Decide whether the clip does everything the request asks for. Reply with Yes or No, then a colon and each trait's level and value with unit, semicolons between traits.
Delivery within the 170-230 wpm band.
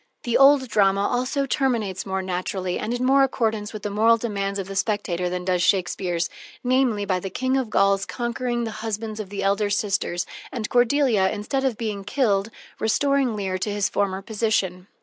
Yes: average, 190 wpm